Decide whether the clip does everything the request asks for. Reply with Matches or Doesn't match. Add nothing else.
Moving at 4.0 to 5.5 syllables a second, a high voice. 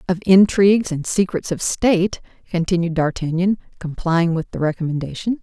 Doesn't match